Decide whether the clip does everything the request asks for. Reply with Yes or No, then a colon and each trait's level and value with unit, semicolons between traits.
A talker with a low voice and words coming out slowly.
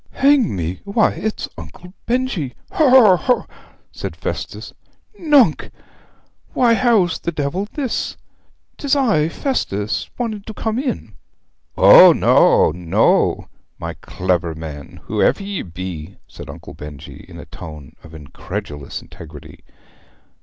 No: medium, 170 Hz; slow, 125 wpm